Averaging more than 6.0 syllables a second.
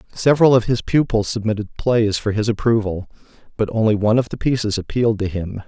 Yes: 6.2 syllables/s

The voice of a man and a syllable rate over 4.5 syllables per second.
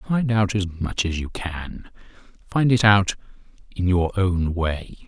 No: male; 3.8 syllables/s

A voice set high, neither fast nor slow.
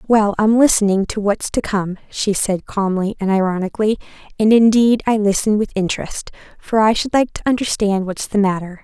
Yes: high, 205 Hz; average, 185 wpm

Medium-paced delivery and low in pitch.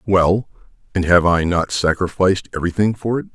Yes: average, 160 wpm; very low, 90 Hz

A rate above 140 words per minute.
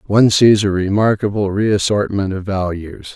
No: slow, 135 wpm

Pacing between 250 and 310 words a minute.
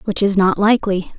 No: fast, 205 wpm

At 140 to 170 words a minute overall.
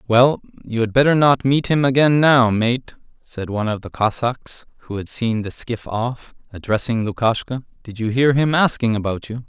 No: average, 190 wpm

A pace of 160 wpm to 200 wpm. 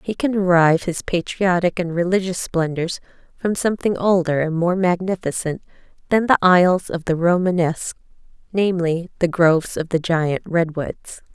No: average, 145 wpm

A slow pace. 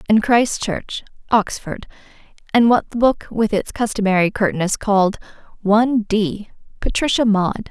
Yes: slow, 130 wpm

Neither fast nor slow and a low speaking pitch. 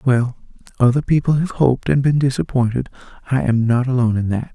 Yes: average, 185 wpm; low, 125 Hz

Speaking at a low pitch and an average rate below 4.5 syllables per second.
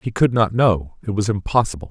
No: low, 105 Hz; 5.7 syllables/s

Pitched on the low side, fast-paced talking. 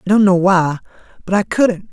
No: high, 190 Hz; fast, 220 wpm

